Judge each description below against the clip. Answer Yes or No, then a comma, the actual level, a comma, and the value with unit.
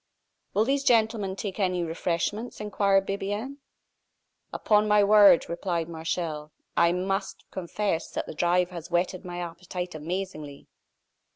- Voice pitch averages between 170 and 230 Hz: Yes, medium, 185 Hz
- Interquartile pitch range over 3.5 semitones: No, average, 3.2 semitones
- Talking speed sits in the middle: No, slow, 125 wpm